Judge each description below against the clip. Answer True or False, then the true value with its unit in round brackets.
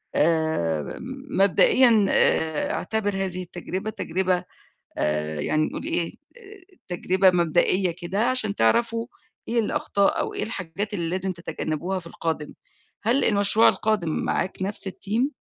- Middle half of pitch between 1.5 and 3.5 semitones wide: False (4.3 semitones)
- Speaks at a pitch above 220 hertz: False (185 Hz)